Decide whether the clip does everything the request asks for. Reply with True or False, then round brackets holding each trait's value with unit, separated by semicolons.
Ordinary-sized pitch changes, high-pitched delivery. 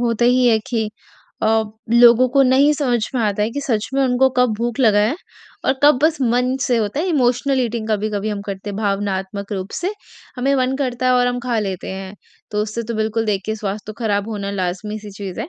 True (3.4 semitones; 225 Hz)